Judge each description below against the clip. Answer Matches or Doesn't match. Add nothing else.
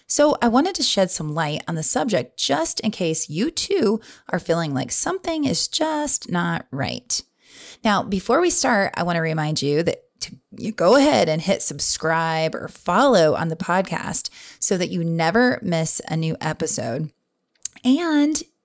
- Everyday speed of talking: Matches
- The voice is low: Doesn't match